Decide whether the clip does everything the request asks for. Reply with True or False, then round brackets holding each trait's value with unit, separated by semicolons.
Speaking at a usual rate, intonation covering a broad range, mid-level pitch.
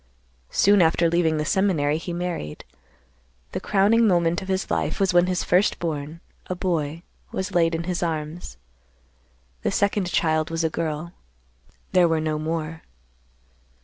False (145 wpm; 2.5 semitones; 170 Hz)